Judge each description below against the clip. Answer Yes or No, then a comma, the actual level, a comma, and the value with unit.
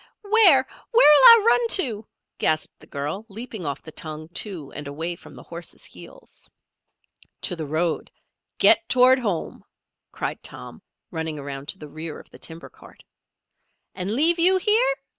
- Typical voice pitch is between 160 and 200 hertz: Yes, medium, 185 Hz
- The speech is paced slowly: No, average, 160 wpm